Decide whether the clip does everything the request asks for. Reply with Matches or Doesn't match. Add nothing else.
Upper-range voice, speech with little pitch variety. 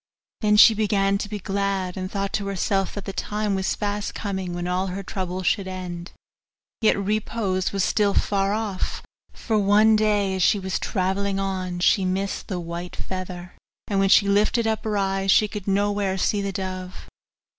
Matches